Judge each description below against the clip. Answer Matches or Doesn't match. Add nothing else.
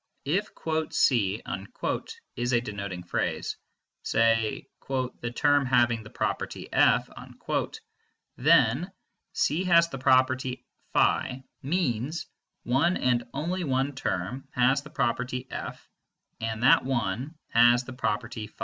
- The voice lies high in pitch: Doesn't match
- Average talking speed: Doesn't match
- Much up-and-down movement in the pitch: Doesn't match